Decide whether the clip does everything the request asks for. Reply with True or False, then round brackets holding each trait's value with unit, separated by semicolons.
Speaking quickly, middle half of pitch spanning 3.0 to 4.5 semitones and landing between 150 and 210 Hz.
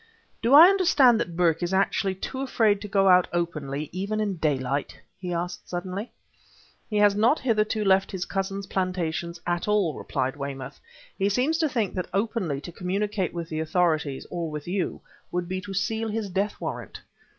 False (180 wpm; 3.6 semitones; 190 Hz)